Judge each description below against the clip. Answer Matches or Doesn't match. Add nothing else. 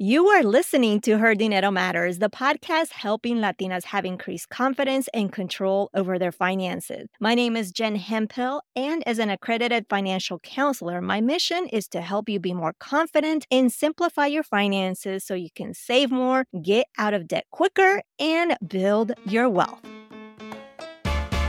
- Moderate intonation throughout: Doesn't match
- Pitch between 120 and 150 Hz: Doesn't match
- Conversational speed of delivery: Matches